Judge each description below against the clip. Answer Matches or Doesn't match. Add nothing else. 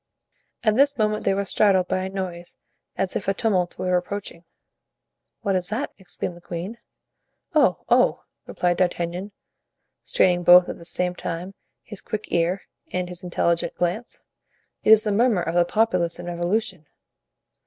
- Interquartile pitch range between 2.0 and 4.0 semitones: Matches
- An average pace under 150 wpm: Doesn't match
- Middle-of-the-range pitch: Matches